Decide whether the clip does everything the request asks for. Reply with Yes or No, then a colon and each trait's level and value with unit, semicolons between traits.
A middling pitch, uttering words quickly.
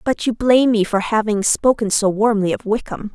No: high, 215 Hz; fast, 210 wpm